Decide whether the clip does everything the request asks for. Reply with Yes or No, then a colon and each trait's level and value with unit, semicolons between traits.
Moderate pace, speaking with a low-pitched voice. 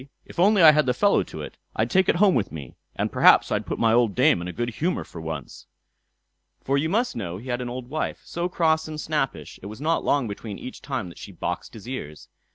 No: fast, 250 wpm; low, 130 Hz